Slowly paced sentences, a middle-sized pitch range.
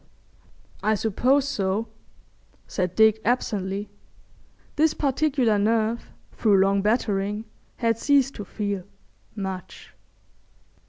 Yes: slow, 95 wpm; average, 3.4 semitones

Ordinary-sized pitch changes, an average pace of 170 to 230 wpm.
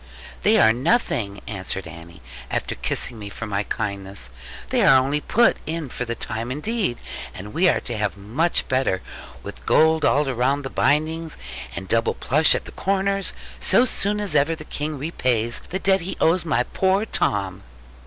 No: wide, 7.1 semitones; average, 180 wpm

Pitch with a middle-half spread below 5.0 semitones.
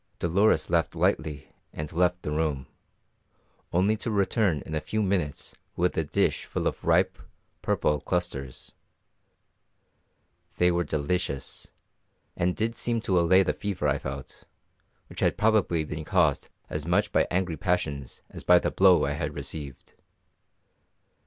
Yes: average, 4.0 semitones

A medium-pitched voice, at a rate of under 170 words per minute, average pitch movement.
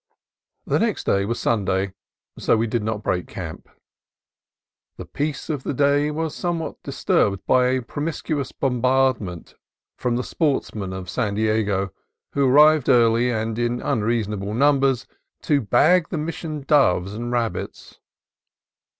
No: low, 120 Hz; average, 140 wpm; average, 5.0 semitones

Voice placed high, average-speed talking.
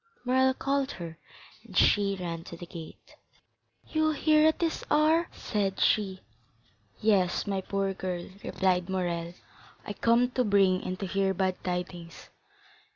Yes: high, 195 Hz; average, 145 wpm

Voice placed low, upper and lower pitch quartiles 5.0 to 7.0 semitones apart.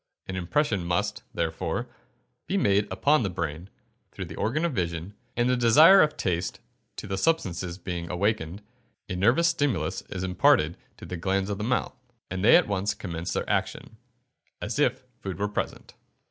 Yes: very low, 95 Hz; average, 5.3 semitones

